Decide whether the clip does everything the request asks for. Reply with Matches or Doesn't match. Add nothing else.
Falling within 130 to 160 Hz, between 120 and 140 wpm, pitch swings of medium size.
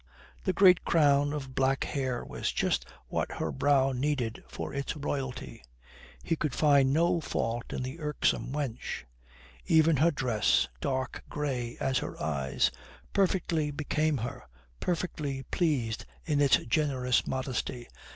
Matches